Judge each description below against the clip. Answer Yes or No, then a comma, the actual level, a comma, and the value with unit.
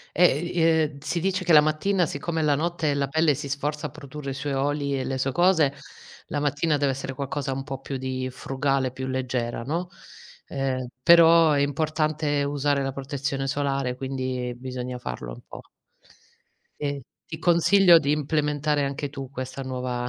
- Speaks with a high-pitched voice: No, medium, 140 Hz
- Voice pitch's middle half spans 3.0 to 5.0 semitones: No, narrow, 2.5 semitones